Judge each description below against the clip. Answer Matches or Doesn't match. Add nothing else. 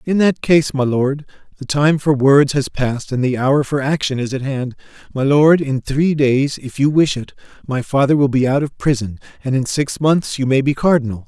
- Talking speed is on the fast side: Matches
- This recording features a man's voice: Matches